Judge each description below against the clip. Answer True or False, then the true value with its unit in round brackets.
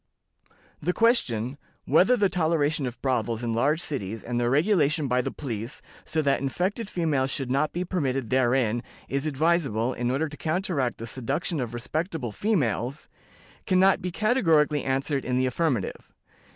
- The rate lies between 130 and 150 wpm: False (160 wpm)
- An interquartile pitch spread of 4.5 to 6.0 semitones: True (5.1 semitones)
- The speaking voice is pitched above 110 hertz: True (140 Hz)